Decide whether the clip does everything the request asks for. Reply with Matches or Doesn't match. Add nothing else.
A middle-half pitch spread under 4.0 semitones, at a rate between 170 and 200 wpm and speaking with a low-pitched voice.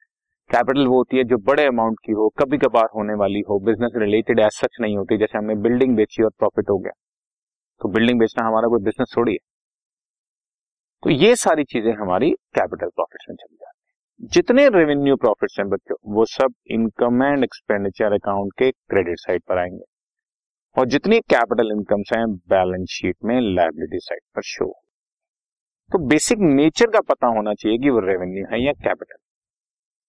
Doesn't match